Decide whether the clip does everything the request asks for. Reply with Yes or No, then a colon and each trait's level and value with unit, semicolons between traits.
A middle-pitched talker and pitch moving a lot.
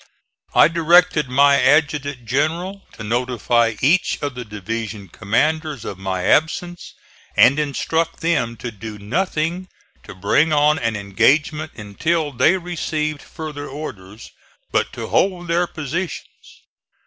Yes: medium, 145 Hz; wide, 5.9 semitones